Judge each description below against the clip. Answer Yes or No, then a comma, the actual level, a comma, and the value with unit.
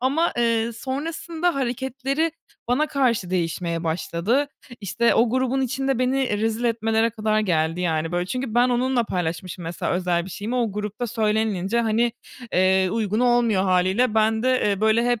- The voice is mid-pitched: No, high, 225 Hz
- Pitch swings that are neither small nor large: Yes, average, 5.0 semitones